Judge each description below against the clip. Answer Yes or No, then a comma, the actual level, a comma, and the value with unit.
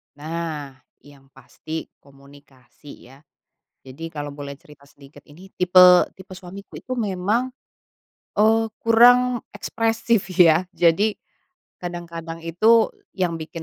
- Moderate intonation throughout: No, wide, 5.9 semitones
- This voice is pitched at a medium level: Yes, medium, 170 Hz